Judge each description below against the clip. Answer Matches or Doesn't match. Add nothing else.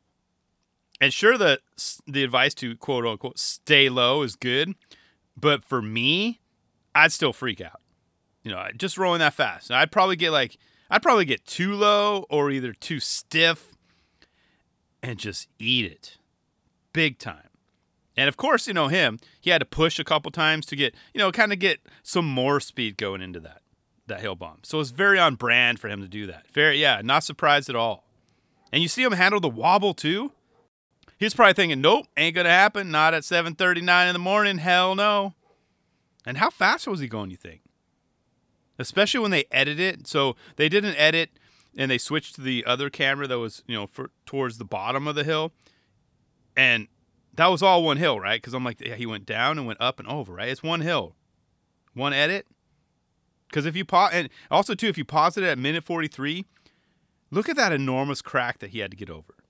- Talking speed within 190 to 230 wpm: Matches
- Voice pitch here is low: Doesn't match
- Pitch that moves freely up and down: Matches